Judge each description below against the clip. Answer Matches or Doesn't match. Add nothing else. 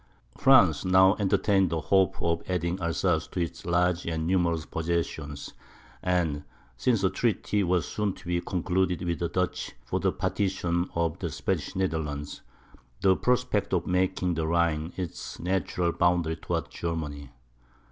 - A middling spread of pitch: Doesn't match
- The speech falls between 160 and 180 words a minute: Doesn't match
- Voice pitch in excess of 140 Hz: Doesn't match